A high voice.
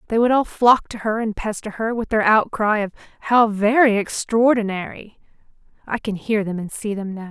Yes: high, 215 Hz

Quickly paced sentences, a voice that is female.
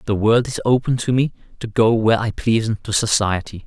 No: fast, 215 wpm; male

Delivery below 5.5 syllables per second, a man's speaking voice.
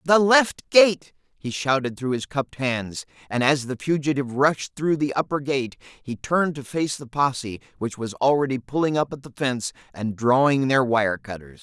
Yes: 5.0 syllables/s; male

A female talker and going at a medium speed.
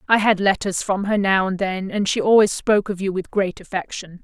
No: female; fast, 240 wpm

